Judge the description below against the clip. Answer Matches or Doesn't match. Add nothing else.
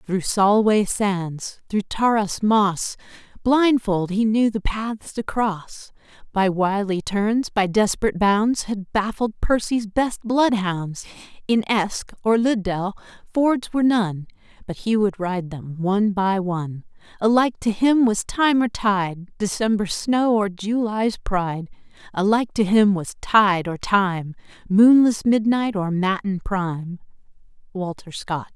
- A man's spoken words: Doesn't match